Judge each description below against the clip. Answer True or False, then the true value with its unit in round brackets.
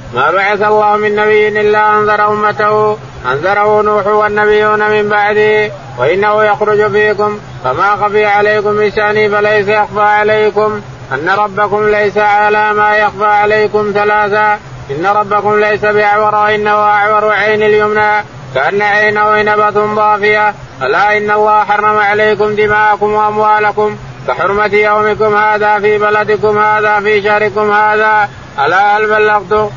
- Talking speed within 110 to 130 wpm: True (125 wpm)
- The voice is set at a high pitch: True (210 Hz)